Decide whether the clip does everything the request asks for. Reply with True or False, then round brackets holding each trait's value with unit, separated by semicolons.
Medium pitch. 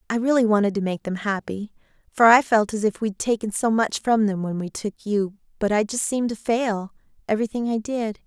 False (215 Hz)